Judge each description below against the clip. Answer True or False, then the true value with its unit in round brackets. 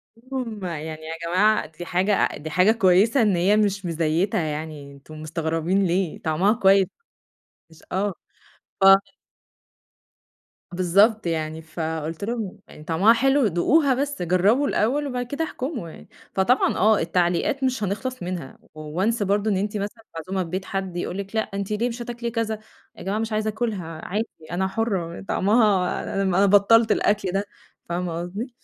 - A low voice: False (195 Hz)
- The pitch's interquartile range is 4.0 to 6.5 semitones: True (4.3 semitones)